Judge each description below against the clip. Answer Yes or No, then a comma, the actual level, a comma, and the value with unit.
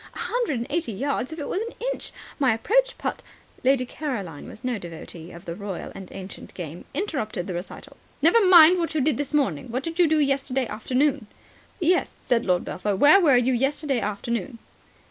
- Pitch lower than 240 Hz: No, very high, 260 Hz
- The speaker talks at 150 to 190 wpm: No, fast, 205 wpm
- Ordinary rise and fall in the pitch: No, wide, 7.2 semitones